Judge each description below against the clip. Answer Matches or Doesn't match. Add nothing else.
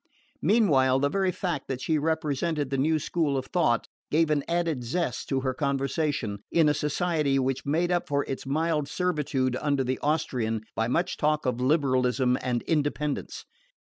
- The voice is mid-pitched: Matches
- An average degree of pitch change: Matches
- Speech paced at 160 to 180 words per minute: Matches